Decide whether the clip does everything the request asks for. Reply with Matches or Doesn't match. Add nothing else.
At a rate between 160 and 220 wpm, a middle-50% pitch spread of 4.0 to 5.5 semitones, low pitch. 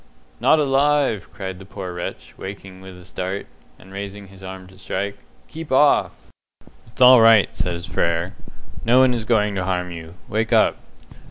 Doesn't match